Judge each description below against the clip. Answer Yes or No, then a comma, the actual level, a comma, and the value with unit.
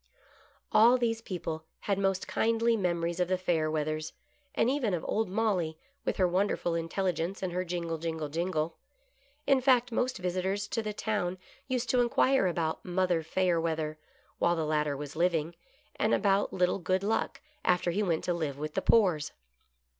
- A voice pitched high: No, medium, 180 Hz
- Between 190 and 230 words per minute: No, average, 170 wpm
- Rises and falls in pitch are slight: No, average, 4.2 semitones